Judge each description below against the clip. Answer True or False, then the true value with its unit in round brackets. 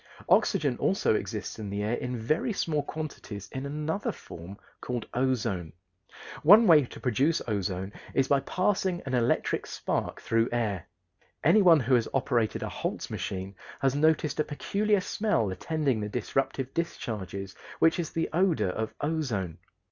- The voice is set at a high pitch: False (130 Hz)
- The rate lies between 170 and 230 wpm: False (150 wpm)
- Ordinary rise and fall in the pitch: False (6.9 semitones)